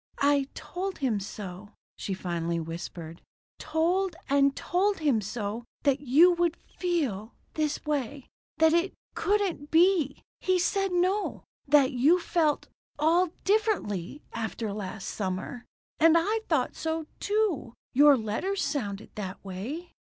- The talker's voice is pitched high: Yes, very high, 290 Hz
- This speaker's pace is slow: Yes, slow, 130 wpm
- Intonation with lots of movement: Yes, wide, 8.6 semitones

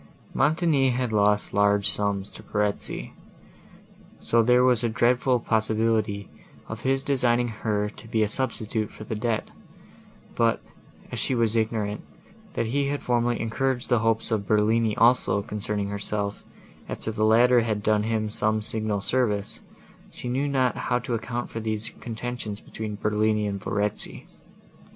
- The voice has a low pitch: Yes, low, 110 Hz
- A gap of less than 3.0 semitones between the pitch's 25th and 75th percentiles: Yes, narrow, 2.6 semitones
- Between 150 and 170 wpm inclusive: Yes, average, 155 wpm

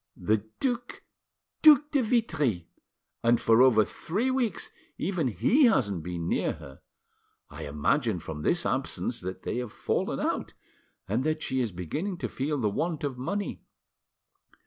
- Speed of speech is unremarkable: Yes, average, 150 wpm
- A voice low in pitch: Yes, low, 130 Hz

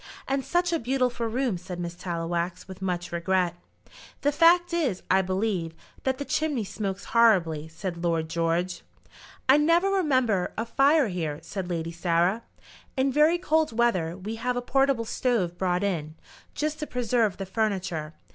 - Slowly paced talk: No, average, 160 wpm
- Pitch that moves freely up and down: Yes, wide, 7.1 semitones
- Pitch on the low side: No, high, 200 Hz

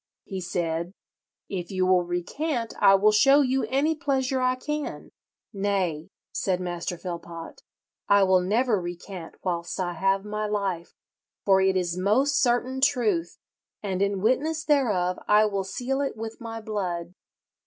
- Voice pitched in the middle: No, high, 200 Hz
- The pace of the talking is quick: No, average, 150 wpm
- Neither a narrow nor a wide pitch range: No, wide, 5.9 semitones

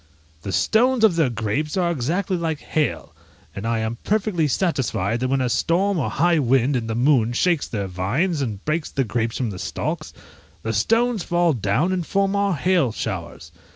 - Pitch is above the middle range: No, medium, 145 Hz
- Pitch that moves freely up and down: Yes, wide, 7.4 semitones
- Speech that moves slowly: No, average, 190 wpm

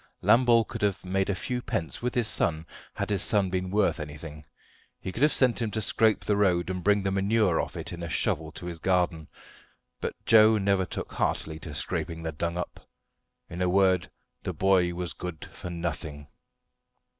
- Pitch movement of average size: Yes, average, 3.4 semitones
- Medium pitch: No, very low, 95 Hz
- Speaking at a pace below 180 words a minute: No, average, 195 wpm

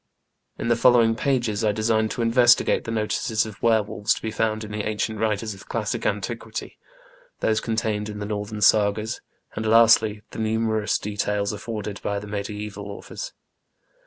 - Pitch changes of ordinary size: No, narrow, 1.4 semitones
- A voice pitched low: Yes, low, 110 Hz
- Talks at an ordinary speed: Yes, average, 165 wpm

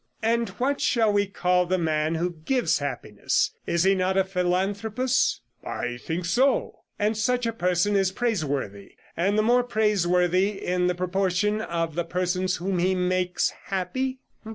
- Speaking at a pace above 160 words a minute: No, average, 155 wpm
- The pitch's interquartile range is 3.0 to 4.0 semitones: Yes, average, 3.4 semitones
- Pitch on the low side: No, medium, 185 Hz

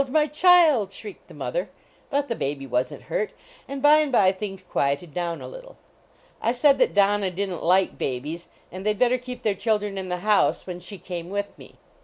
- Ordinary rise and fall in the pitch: No, wide, 6.5 semitones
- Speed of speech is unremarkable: No, fast, 225 wpm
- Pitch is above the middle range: Yes, high, 205 Hz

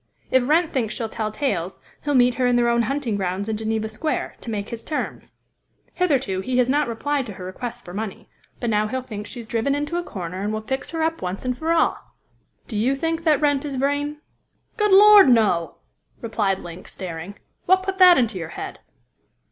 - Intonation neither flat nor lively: No, wide, 5.7 semitones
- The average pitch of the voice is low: No, high, 240 Hz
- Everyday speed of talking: No, fast, 210 wpm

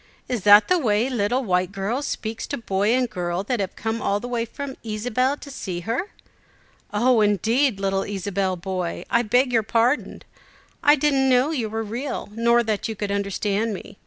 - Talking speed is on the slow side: No, average, 190 wpm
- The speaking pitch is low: No, high, 225 Hz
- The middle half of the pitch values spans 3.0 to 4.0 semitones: Yes, average, 3.7 semitones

